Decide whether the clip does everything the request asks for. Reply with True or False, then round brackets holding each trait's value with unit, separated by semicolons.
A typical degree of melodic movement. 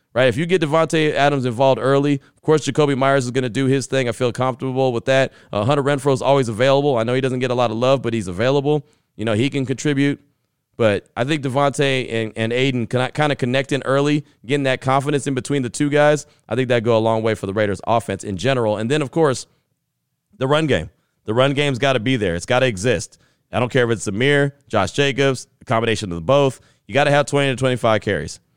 True (3.2 semitones)